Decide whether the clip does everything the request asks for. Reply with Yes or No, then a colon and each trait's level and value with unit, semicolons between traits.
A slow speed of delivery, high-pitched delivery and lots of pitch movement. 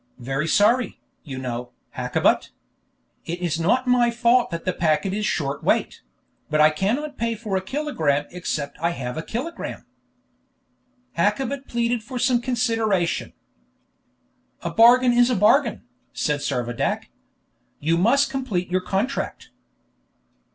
Yes: slow, 130 wpm; high, 210 Hz; wide, 7.2 semitones